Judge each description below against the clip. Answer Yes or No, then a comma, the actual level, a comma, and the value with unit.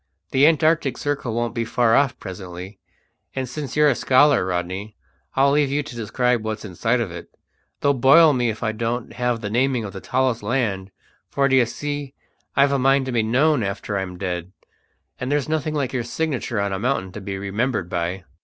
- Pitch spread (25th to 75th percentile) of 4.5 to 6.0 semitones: Yes, average, 5.2 semitones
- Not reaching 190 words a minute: No, average, 200 wpm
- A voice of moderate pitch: No, low, 120 Hz